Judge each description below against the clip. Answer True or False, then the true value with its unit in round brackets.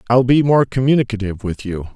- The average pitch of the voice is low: True (115 Hz)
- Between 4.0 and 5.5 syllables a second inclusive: False (6.4 syllables/s)